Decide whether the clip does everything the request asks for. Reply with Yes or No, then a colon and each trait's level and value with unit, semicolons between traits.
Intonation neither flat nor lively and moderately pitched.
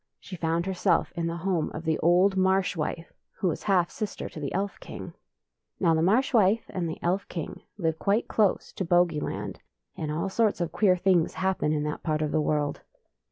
Yes: average, 3.1 semitones; medium, 175 Hz